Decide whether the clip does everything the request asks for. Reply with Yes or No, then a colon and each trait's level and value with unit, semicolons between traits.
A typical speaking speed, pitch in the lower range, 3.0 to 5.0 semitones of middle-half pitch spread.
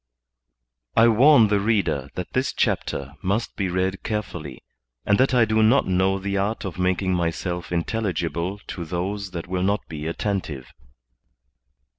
Yes: average, 155 wpm; very low, 95 Hz; average, 3.5 semitones